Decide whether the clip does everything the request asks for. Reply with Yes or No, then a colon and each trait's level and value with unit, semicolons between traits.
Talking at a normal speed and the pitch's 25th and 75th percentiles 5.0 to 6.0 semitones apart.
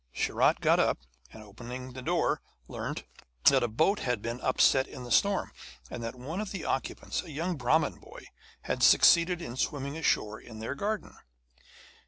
Yes: average, 175 wpm; wide, 5.6 semitones